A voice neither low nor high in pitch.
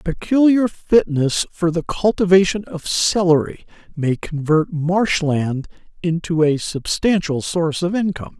Yes: medium, 170 Hz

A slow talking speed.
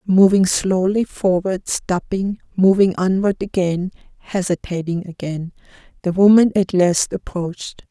Yes: slow, 75 wpm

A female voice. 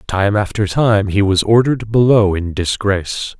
No: male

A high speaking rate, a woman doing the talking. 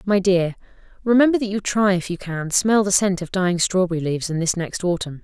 Yes: fast, 230 wpm; female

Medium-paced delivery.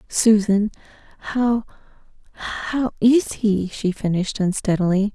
No: slow, 80 wpm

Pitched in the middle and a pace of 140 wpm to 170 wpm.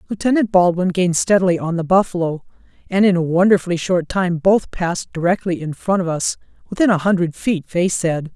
No: medium, 180 Hz; average, 180 wpm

